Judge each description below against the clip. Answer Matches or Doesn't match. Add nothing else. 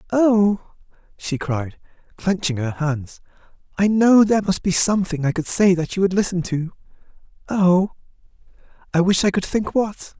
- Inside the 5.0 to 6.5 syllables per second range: Doesn't match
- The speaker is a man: Matches